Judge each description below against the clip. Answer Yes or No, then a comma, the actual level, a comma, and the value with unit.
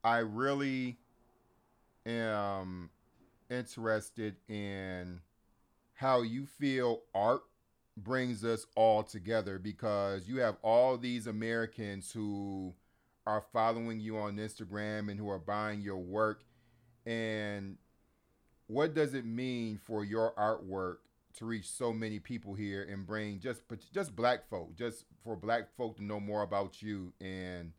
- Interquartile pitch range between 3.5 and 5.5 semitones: No, average, 2.8 semitones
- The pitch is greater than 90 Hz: Yes, low, 110 Hz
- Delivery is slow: Yes, slow, 130 wpm